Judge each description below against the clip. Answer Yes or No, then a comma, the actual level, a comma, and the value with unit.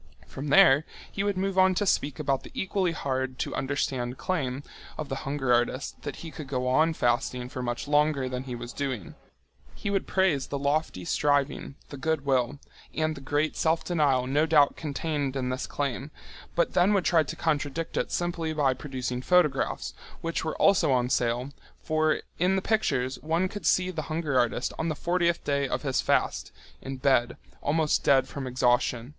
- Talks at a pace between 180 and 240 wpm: Yes, average, 185 wpm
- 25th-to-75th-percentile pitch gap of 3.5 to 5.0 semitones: Yes, average, 3.8 semitones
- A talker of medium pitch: Yes, medium, 145 Hz